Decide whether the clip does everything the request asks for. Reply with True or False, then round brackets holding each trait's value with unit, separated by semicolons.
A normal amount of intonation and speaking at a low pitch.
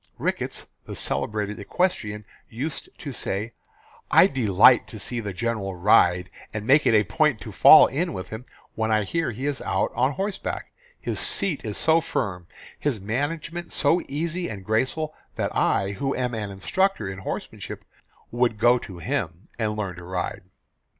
False (6.1 semitones; 110 Hz)